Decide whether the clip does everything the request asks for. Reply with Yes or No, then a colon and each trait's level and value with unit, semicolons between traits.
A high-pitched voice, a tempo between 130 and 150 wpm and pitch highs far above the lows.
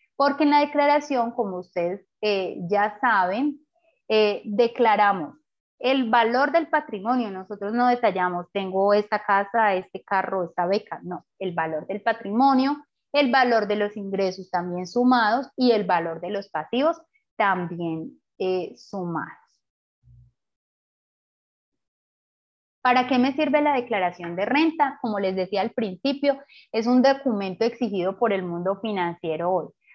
Yes: high, 210 Hz; average, 135 wpm; wide, 5.9 semitones